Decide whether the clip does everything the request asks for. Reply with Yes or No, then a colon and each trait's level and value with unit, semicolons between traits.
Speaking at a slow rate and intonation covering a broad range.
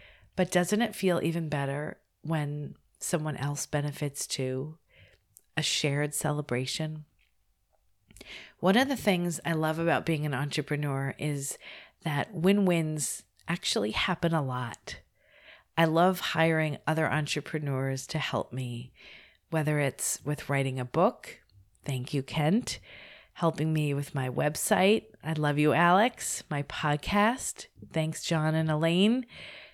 No: slow, 130 wpm; average, 3.0 semitones